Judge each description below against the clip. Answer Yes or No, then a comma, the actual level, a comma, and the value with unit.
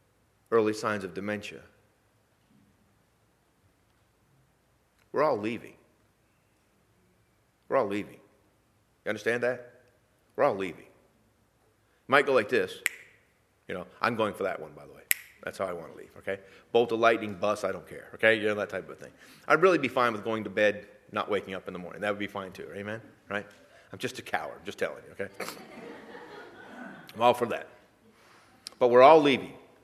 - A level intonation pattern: No, average, 3.4 semitones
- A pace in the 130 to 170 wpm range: No, average, 180 wpm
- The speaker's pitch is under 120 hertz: Yes, low, 110 Hz